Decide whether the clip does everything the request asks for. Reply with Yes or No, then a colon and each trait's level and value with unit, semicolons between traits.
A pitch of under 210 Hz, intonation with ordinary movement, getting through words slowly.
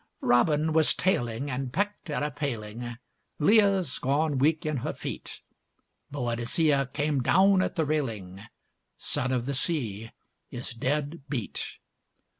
Yes: medium, 140 Hz; average, 4.4 semitones; slow, 130 wpm